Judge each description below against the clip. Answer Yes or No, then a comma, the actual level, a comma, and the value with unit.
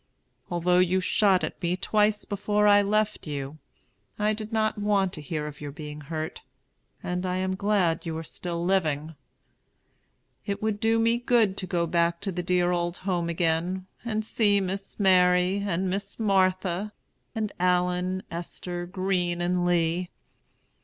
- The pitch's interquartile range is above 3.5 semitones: No, average, 2.8 semitones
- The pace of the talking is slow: No, average, 155 wpm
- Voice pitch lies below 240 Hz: Yes, medium, 185 Hz